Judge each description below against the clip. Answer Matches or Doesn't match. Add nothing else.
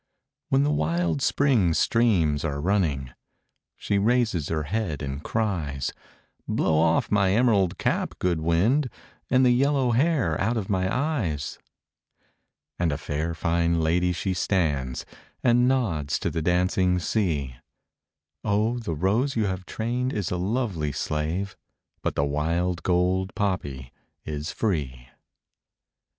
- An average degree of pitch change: Doesn't match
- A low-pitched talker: Matches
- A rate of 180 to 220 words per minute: Doesn't match